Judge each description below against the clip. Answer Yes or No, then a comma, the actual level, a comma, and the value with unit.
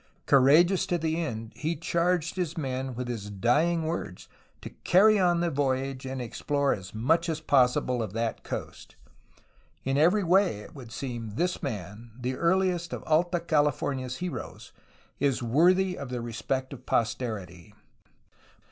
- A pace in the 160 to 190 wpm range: No, average, 150 wpm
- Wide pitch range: Yes, wide, 5.8 semitones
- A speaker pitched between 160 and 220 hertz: No, medium, 140 Hz